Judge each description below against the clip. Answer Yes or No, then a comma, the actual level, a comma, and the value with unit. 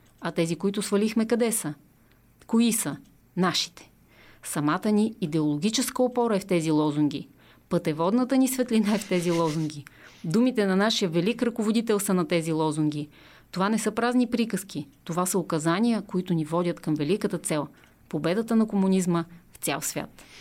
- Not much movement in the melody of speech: No, average, 5.3 semitones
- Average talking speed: Yes, average, 155 wpm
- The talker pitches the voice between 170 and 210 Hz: Yes, medium, 185 Hz